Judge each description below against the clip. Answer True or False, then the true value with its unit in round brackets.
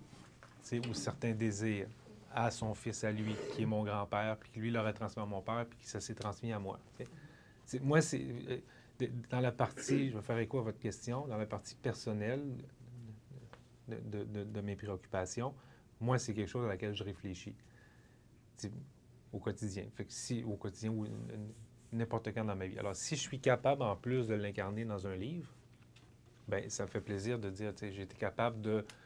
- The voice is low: True (110 Hz)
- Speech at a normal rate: True (200 wpm)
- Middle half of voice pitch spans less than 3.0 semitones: True (2.6 semitones)